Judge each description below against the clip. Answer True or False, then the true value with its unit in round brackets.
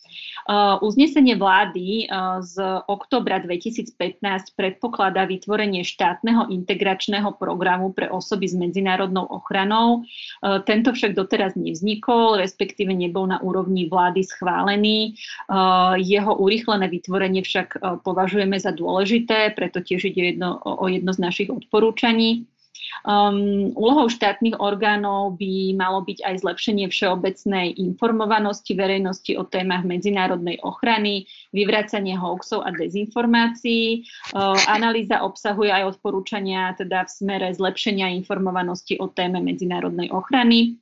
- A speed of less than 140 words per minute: True (120 wpm)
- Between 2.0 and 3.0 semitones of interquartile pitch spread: True (2.4 semitones)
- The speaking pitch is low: False (195 Hz)